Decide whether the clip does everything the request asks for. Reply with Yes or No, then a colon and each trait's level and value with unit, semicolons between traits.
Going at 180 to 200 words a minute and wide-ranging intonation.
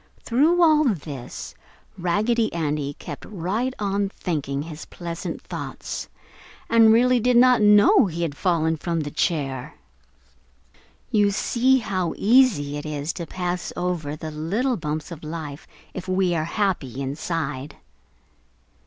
No: slow, 135 wpm; wide, 6.0 semitones